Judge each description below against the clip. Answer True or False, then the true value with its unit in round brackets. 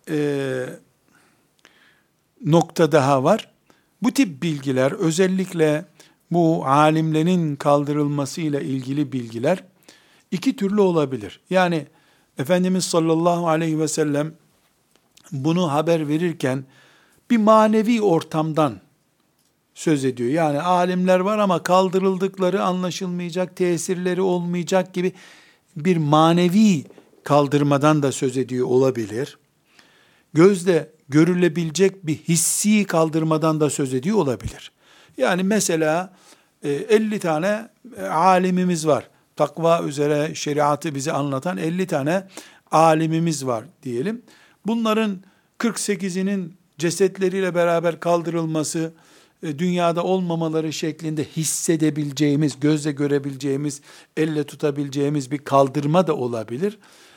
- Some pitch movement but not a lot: True (3.8 semitones)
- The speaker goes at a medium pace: False (90 wpm)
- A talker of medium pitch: True (160 Hz)